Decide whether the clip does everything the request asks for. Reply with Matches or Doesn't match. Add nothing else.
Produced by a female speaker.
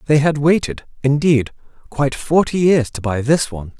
Doesn't match